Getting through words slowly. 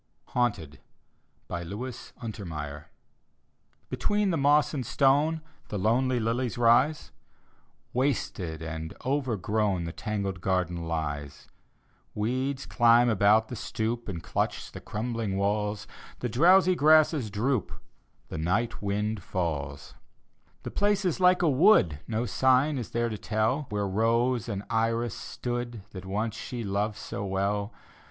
Yes: slow, 130 wpm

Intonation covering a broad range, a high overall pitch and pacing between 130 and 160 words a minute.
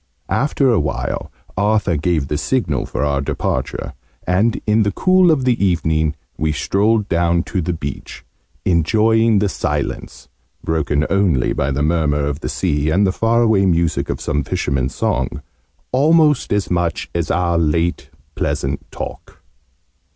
No: wide, 6.0 semitones; very low, 85 Hz; average, 150 wpm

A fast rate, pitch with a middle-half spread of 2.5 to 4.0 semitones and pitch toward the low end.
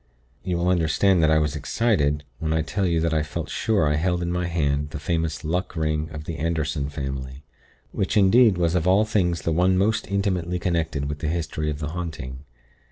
Yes: fast, 210 wpm; average, 2.9 semitones; very low, 80 Hz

